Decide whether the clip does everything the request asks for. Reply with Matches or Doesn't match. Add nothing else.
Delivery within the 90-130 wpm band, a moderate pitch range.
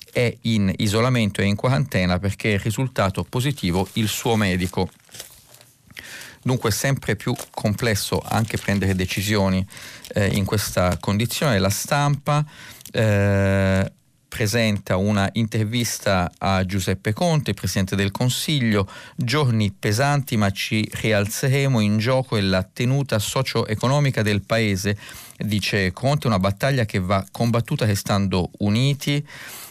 Matches